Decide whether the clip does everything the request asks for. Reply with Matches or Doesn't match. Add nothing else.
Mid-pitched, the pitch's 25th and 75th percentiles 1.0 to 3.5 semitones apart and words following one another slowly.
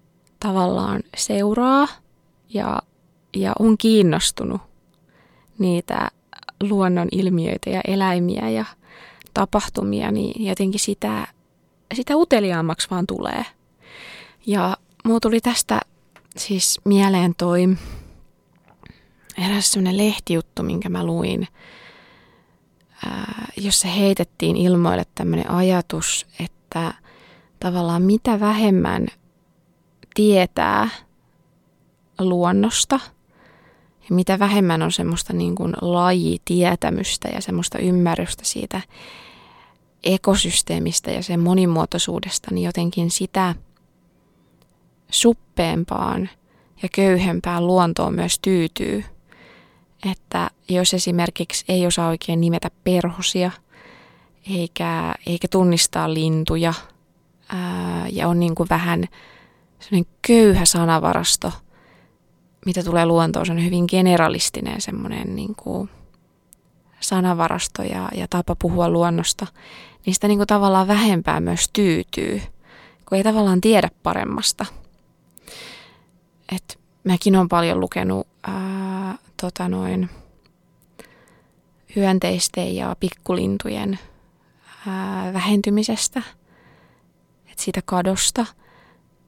Matches